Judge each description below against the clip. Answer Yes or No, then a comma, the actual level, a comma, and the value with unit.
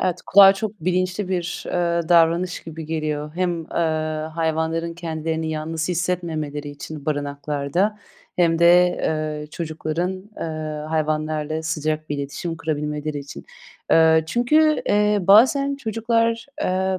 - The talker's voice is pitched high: No, medium, 165 Hz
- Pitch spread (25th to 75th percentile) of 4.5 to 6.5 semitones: No, average, 3.0 semitones